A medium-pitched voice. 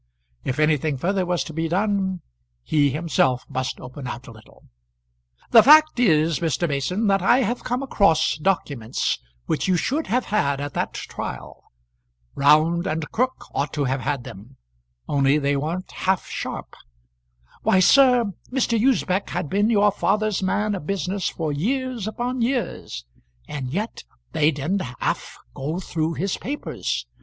Yes: medium, 175 Hz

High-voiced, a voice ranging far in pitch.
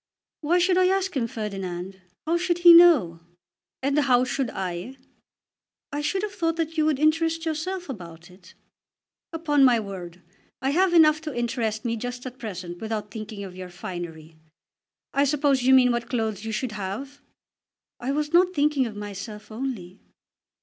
Yes: very high, 250 Hz; wide, 7.3 semitones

